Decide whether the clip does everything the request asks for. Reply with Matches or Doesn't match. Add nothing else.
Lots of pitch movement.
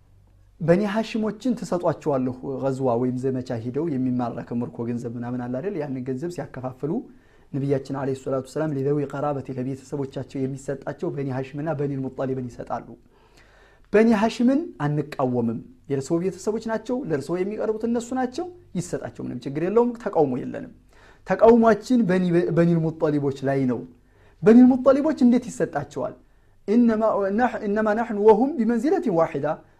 Matches